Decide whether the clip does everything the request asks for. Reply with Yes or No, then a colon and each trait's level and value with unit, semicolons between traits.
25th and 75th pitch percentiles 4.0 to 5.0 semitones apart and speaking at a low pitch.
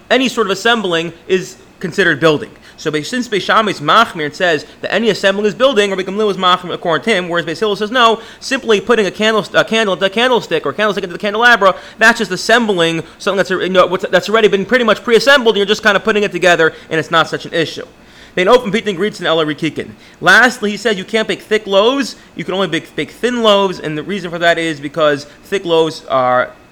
No: average, 4.7 semitones; high, 195 Hz